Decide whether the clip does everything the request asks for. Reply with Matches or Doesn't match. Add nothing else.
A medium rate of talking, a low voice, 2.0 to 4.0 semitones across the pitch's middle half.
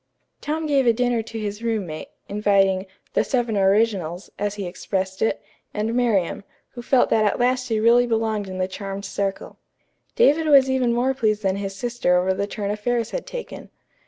Doesn't match